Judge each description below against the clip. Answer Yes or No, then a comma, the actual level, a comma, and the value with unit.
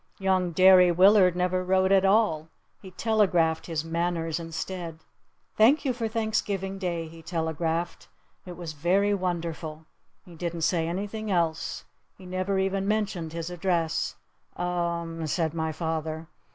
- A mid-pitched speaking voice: Yes, medium, 175 Hz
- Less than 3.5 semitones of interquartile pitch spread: Yes, average, 2.7 semitones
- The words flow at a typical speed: Yes, average, 145 wpm